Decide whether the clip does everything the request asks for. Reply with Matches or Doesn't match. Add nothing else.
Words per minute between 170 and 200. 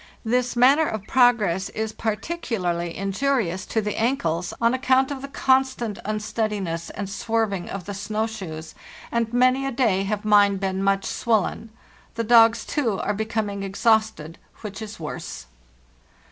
Doesn't match